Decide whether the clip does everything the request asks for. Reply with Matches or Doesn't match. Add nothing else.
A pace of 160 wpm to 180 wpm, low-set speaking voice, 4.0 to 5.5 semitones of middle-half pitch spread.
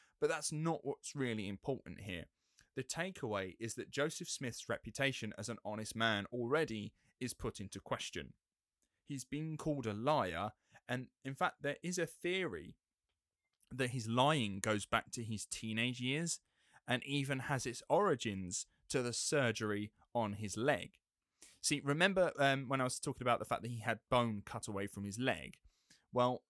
Matches